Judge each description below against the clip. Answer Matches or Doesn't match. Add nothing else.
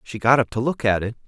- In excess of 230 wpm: Matches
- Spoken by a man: Matches